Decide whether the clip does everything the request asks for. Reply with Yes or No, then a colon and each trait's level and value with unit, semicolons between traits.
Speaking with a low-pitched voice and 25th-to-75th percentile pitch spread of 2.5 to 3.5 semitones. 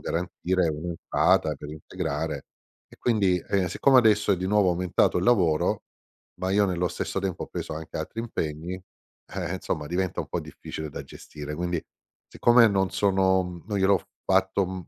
Yes: very low, 90 Hz; average, 2.9 semitones